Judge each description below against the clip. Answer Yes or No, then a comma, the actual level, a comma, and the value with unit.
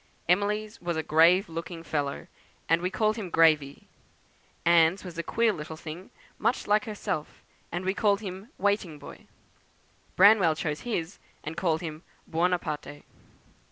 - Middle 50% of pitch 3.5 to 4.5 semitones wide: Yes, average, 4.1 semitones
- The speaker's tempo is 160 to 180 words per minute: No, average, 145 wpm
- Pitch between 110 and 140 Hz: No, medium, 175 Hz